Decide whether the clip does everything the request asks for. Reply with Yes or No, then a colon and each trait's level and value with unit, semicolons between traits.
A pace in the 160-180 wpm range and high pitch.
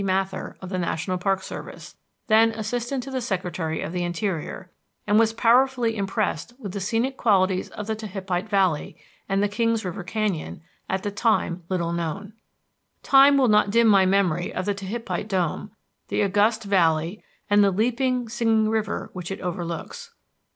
Yes: average, 165 wpm; high, 200 Hz